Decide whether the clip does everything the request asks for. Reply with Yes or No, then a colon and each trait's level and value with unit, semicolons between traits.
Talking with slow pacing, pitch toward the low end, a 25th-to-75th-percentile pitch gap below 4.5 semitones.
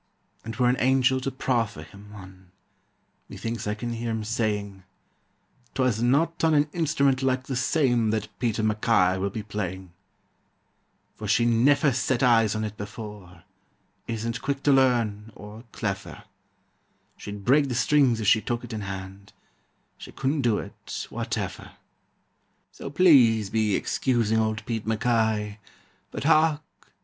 No: average, 145 wpm; low, 115 Hz; average, 3.8 semitones